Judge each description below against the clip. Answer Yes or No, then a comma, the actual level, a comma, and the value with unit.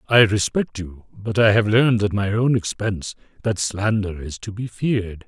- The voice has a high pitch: No, low, 105 Hz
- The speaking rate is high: No, average, 195 wpm